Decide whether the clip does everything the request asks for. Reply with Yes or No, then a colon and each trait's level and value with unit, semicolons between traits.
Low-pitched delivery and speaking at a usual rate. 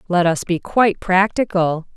No: medium, 185 Hz; average, 155 wpm